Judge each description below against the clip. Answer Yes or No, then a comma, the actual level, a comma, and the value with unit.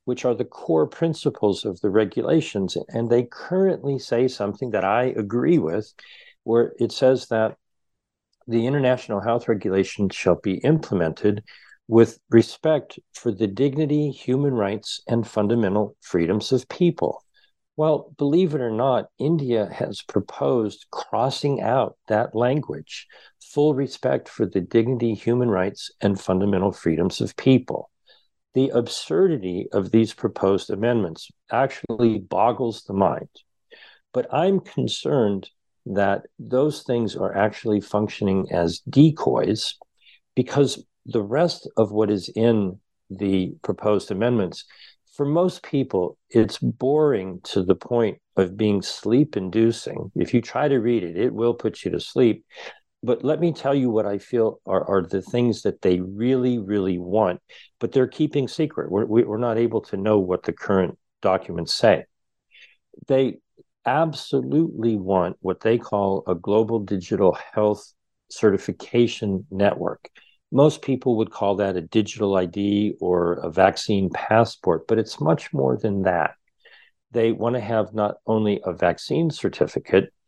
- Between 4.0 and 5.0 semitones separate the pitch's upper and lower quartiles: Yes, average, 4.6 semitones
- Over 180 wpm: No, average, 140 wpm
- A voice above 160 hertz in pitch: No, low, 115 Hz